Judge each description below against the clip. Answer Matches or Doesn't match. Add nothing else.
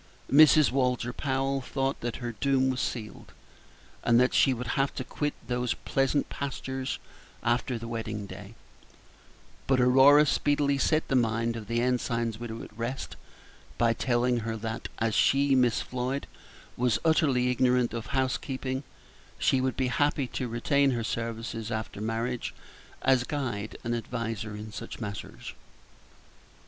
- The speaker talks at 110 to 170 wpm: Matches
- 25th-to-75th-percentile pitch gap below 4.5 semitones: Matches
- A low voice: Matches